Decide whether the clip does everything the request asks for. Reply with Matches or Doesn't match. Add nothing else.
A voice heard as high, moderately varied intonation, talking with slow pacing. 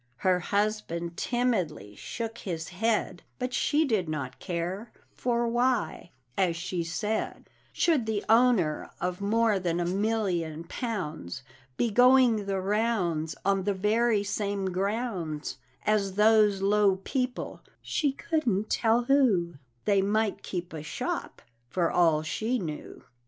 Matches